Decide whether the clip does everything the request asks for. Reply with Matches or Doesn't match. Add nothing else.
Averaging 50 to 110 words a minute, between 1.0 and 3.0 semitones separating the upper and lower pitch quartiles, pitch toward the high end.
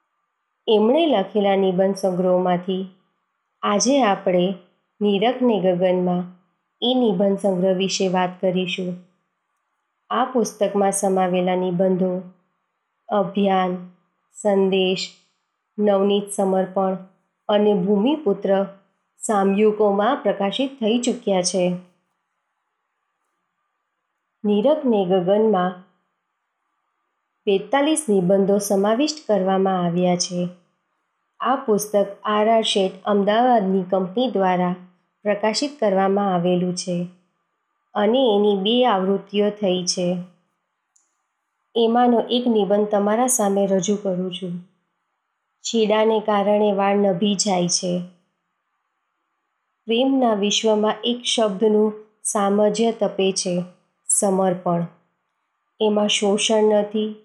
Matches